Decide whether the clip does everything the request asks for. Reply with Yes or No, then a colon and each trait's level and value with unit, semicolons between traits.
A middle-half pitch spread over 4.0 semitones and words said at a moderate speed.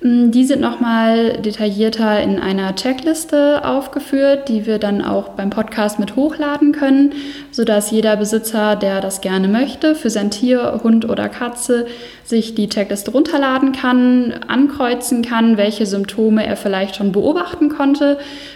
Yes: average, 4.6 semitones; average, 140 wpm